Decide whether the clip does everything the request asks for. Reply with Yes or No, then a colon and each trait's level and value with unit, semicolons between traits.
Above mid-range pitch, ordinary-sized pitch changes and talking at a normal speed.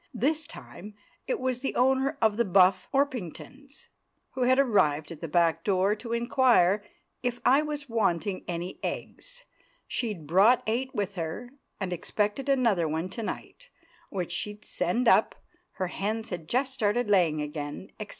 No: high, 210 Hz; wide, 6.4 semitones; average, 150 wpm